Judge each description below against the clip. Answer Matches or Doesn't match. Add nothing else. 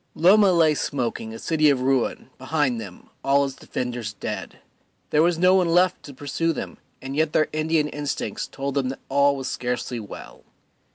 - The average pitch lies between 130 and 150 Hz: Matches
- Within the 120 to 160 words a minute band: Doesn't match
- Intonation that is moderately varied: Matches